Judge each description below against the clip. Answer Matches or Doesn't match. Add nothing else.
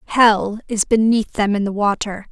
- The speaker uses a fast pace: Doesn't match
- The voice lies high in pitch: Matches